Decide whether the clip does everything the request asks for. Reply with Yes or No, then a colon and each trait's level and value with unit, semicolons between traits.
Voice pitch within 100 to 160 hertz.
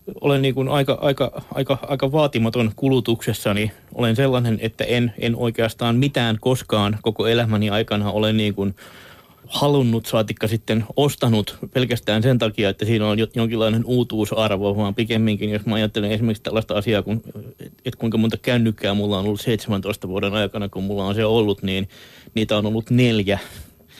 Yes: low, 110 Hz